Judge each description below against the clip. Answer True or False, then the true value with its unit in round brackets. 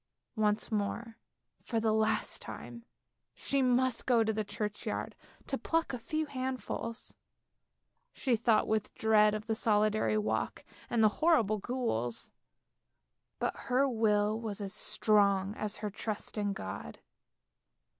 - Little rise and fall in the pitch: True (2.3 semitones)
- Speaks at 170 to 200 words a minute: False (135 wpm)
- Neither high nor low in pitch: False (220 Hz)